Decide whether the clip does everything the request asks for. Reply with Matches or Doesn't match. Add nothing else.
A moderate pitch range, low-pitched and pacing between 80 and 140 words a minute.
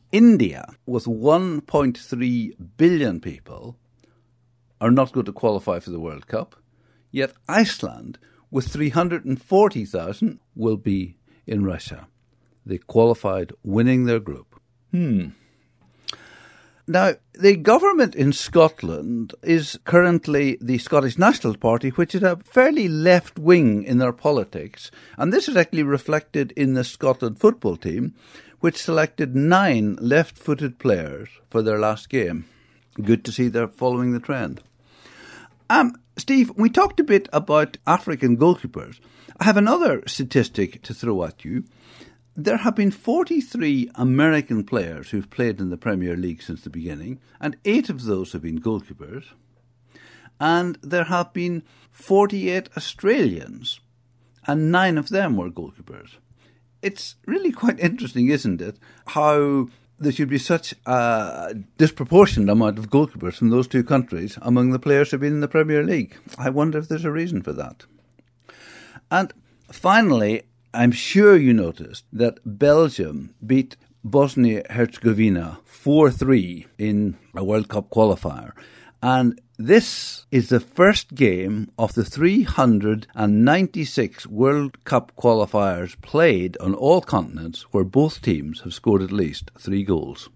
Doesn't match